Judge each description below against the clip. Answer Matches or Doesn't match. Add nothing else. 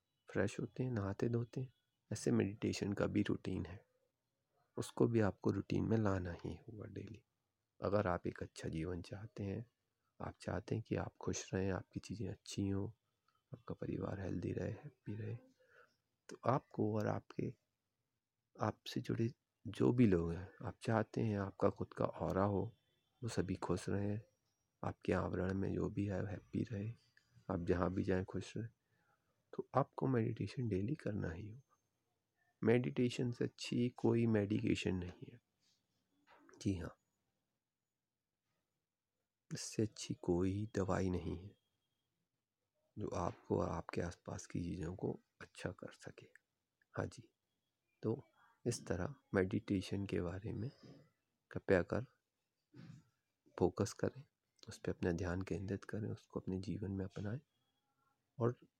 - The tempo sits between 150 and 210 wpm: Doesn't match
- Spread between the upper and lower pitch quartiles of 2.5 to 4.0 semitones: Matches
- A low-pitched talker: Matches